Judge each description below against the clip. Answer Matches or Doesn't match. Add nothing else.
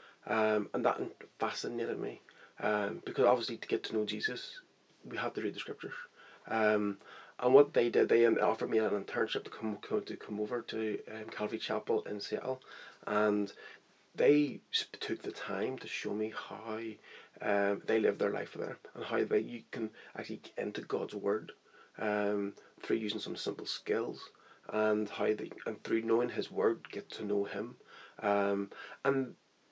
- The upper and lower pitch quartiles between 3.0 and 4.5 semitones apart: Doesn't match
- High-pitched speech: Doesn't match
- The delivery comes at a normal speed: Matches